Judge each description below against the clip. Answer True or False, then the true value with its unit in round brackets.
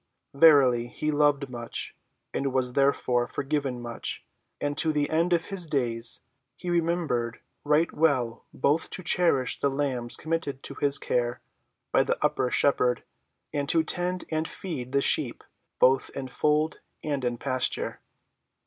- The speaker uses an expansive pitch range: False (4.0 semitones)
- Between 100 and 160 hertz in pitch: True (140 Hz)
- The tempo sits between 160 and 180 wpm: False (150 wpm)